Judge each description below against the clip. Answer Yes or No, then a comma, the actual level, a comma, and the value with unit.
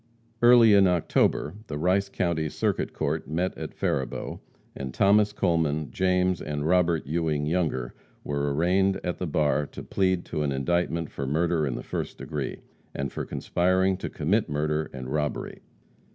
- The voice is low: Yes, very low, 80 Hz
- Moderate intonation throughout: Yes, average, 3.9 semitones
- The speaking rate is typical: Yes, average, 160 wpm